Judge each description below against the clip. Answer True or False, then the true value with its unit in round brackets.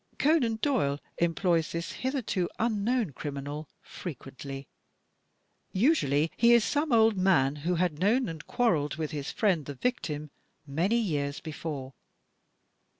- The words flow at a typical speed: False (130 wpm)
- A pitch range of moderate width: False (7.7 semitones)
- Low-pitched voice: False (170 Hz)